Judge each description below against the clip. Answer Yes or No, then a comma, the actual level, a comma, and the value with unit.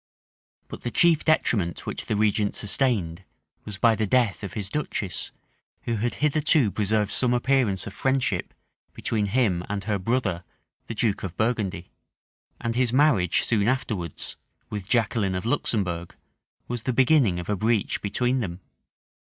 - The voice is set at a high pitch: No, low, 110 Hz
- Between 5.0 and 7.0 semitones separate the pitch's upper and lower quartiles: No, average, 4.1 semitones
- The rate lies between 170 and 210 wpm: No, average, 150 wpm